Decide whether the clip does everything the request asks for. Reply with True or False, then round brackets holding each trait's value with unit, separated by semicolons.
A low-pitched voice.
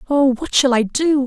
False (270 Hz)